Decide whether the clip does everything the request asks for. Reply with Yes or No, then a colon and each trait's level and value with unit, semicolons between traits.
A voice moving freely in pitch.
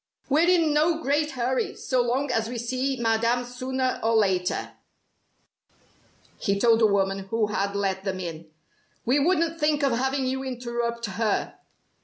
No: average, 4.1 semitones